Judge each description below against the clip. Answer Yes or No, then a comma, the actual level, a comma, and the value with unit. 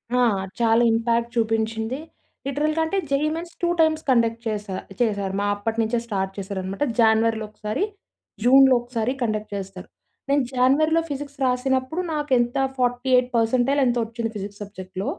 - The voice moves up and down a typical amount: Yes, average, 3.5 semitones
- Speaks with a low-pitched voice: No, high, 235 Hz